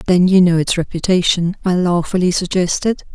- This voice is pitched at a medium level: Yes, medium, 180 Hz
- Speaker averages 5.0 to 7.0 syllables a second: Yes, 5.4 syllables/s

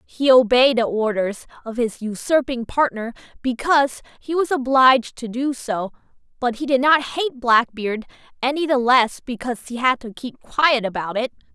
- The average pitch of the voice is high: Yes, very high, 250 Hz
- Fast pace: No, average, 165 wpm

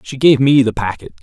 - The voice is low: Yes, low, 125 Hz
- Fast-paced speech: Yes, fast, 245 wpm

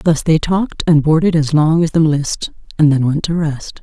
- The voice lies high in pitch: No, medium, 155 Hz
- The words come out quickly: Yes, fast, 235 wpm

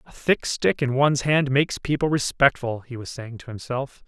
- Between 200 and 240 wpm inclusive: Yes, fast, 205 wpm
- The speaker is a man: Yes, male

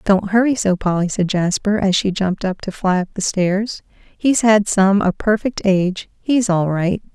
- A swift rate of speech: No, average, 185 wpm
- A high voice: Yes, high, 195 Hz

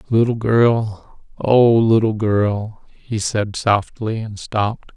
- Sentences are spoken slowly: Yes, slow, 110 wpm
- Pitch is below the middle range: Yes, low, 110 Hz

